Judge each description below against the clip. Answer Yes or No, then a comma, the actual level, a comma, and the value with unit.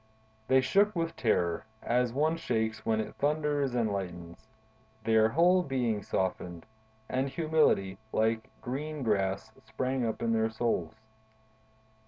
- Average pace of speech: No, slow, 130 wpm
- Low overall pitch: Yes, low, 115 Hz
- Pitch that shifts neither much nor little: Yes, average, 4.7 semitones